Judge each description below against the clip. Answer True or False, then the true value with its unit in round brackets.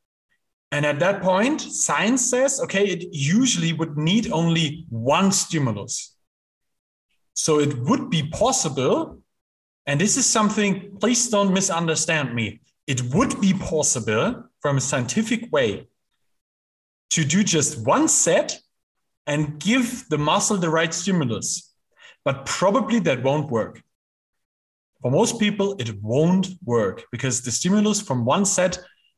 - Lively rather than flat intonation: True (6.7 semitones)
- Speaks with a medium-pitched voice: True (165 Hz)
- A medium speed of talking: False (130 wpm)